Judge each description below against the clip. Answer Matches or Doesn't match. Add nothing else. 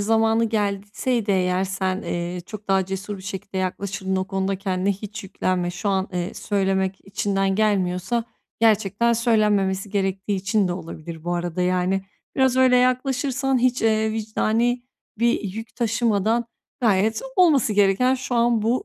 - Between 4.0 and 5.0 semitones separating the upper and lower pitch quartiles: Doesn't match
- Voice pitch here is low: Doesn't match